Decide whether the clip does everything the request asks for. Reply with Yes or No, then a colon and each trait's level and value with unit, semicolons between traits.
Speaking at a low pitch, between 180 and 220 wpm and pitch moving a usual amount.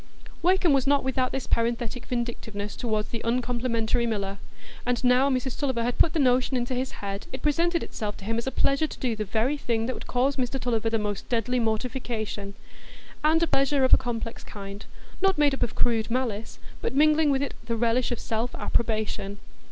No: high, 245 Hz; average, 200 wpm; average, 3.0 semitones